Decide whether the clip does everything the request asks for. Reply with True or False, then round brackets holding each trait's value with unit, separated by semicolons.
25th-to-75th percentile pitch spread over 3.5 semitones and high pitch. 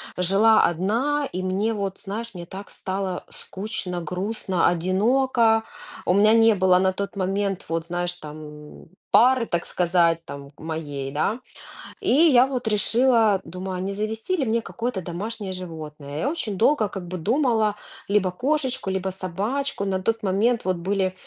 True (4.1 semitones; 195 Hz)